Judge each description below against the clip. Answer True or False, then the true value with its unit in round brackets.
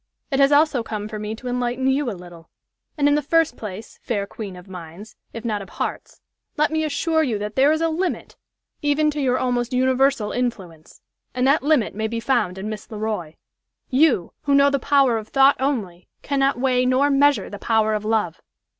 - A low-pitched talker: False (245 Hz)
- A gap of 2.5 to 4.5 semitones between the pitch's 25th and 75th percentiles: False (4.9 semitones)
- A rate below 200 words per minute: False (205 wpm)